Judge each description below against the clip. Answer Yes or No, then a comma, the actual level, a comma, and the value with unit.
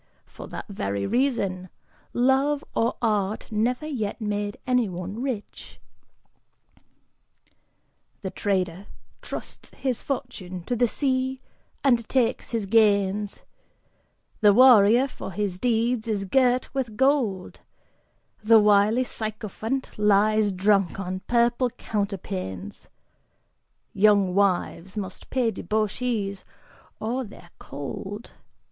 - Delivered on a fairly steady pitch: No, average, 3.9 semitones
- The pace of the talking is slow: Yes, slow, 100 wpm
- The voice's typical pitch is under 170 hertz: No, high, 215 Hz